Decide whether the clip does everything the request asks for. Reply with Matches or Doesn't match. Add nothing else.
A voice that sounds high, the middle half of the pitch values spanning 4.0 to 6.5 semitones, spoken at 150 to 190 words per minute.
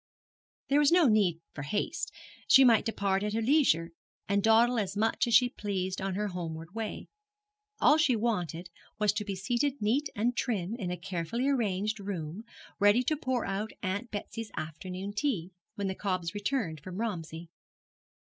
Matches